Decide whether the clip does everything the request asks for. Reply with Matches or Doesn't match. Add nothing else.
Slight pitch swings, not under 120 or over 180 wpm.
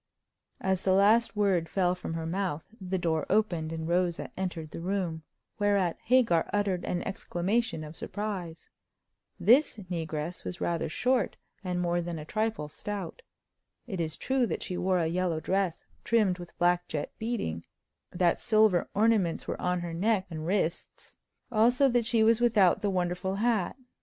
Doesn't match